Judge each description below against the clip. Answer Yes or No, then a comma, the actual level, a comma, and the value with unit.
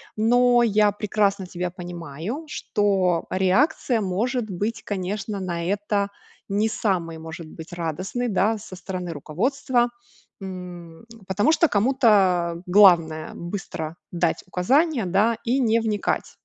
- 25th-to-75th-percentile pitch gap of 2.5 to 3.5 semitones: No, average, 4.1 semitones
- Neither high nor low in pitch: No, high, 195 Hz